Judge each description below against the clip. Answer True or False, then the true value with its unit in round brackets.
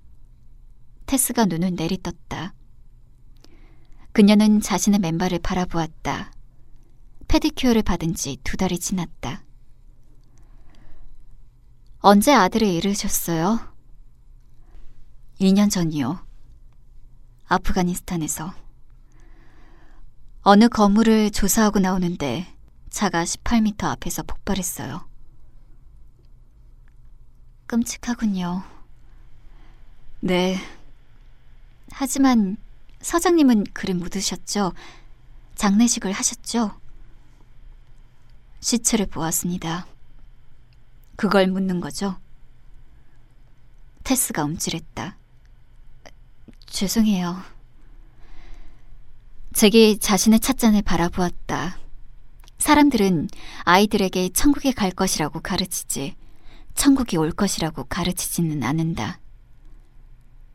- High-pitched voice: False (180 Hz)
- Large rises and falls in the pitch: True (8.3 semitones)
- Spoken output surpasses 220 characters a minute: False (180 characters per minute)